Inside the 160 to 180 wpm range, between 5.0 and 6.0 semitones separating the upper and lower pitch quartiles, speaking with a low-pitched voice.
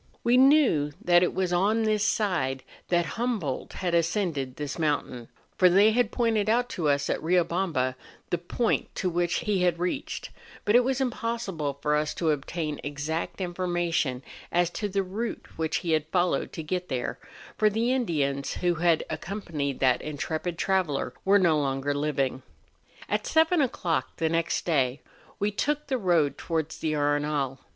No: average, 170 wpm; wide, 5.4 semitones; medium, 175 Hz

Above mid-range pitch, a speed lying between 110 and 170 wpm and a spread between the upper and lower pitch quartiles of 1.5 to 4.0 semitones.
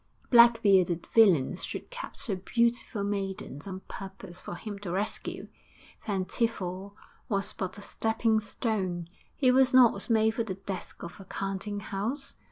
Yes: high, 200 Hz; average, 150 wpm; average, 3.2 semitones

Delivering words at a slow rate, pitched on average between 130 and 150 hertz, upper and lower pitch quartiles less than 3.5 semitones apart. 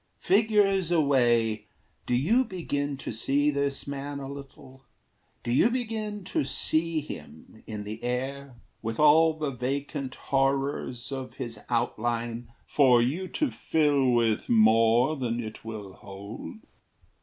No: slow, 130 wpm; low, 135 Hz; average, 4.3 semitones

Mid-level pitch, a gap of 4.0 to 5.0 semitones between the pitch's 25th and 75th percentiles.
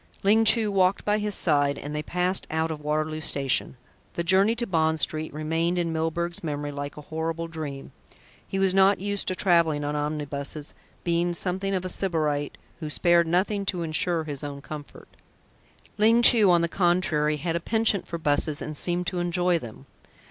No: medium, 165 Hz; average, 3.4 semitones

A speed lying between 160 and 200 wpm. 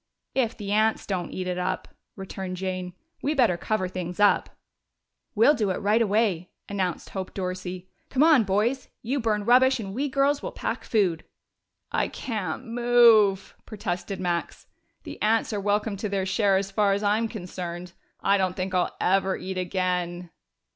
Yes: average, 170 wpm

